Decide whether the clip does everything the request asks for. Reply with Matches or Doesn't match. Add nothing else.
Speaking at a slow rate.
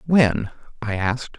Matches